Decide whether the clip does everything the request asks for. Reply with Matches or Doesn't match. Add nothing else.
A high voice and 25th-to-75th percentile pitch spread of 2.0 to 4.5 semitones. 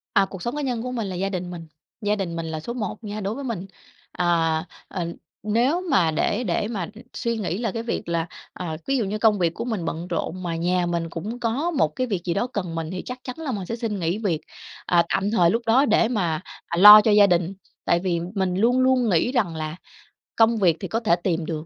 Doesn't match